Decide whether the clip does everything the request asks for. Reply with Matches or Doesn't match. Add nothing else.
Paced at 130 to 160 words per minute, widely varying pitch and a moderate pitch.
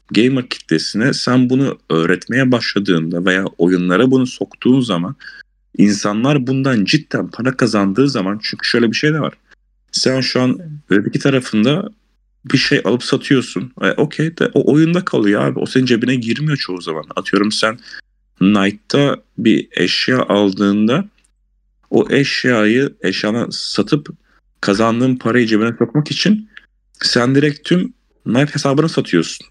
Doesn't match